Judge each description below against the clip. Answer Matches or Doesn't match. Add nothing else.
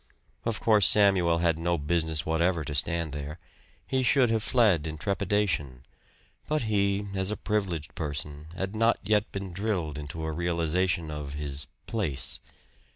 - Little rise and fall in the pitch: Doesn't match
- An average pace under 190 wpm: Matches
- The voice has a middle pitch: Doesn't match